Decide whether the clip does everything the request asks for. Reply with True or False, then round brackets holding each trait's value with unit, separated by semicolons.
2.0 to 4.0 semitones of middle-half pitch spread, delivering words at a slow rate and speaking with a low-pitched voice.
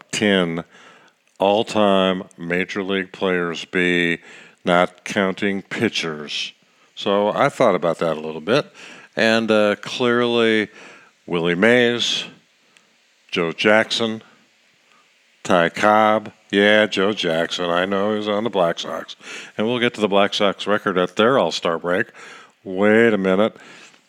True (3.1 semitones; 130 wpm; 100 Hz)